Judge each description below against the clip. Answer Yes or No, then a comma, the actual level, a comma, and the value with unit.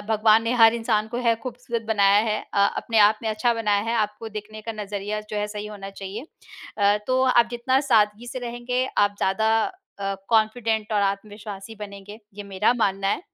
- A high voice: Yes, high, 215 Hz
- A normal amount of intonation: No, narrow, 2.0 semitones